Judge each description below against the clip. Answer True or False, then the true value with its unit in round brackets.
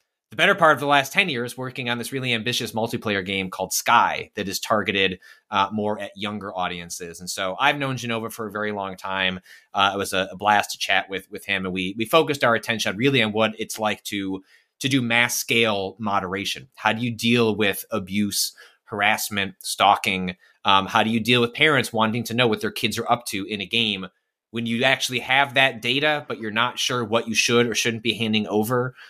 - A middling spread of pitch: True (3.4 semitones)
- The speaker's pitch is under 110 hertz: False (115 Hz)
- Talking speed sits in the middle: False (220 wpm)